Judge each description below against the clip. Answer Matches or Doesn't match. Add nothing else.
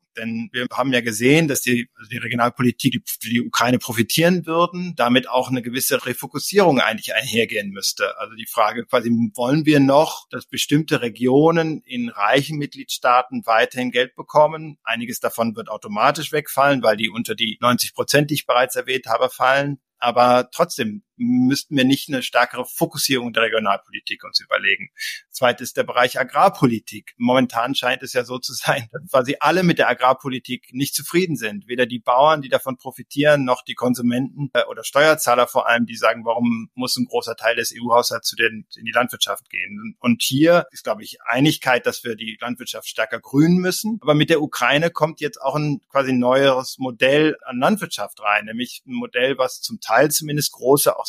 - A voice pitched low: Matches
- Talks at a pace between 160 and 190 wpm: Matches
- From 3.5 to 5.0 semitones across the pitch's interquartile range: Matches